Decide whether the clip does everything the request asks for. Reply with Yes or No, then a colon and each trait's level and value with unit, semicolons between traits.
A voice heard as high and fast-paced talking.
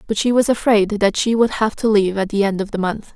Yes: high, 210 Hz; fast, 305 wpm